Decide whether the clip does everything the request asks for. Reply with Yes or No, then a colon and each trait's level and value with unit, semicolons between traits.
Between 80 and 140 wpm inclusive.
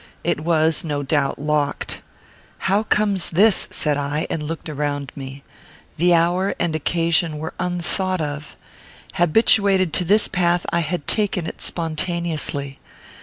Yes: slow, 135 wpm